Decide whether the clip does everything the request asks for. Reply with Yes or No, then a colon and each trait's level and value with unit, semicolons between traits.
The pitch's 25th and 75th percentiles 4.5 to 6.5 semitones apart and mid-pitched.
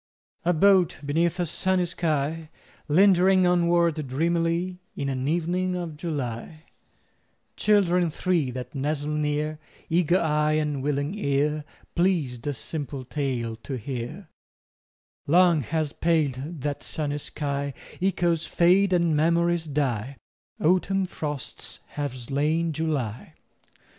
No: average, 3.4 semitones; medium, 155 Hz